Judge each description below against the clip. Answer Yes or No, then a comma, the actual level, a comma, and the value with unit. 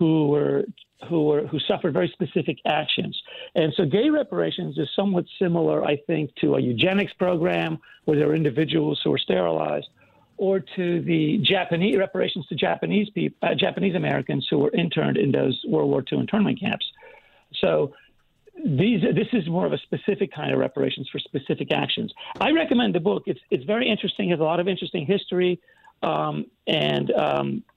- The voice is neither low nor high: Yes, medium, 180 Hz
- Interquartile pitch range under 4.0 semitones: No, average, 4.8 semitones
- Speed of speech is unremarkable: Yes, average, 175 wpm